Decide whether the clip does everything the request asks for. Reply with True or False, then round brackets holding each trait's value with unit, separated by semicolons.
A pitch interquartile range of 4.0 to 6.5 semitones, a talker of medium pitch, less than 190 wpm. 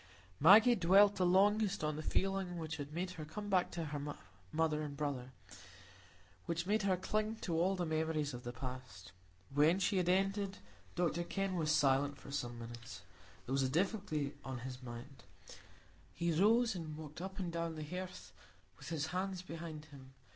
True (4.7 semitones; 165 Hz; 180 wpm)